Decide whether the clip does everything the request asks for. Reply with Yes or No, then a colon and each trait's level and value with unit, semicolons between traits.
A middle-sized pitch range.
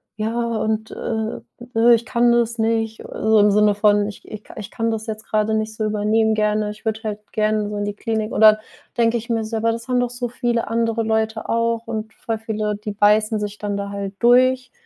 No: narrow, 1.4 semitones